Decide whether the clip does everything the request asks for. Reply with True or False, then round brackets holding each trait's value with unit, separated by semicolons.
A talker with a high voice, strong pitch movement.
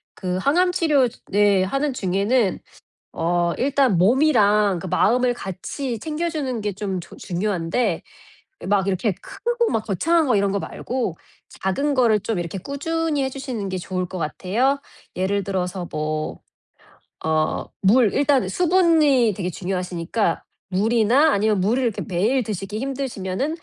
True (210 Hz; 6.3 semitones)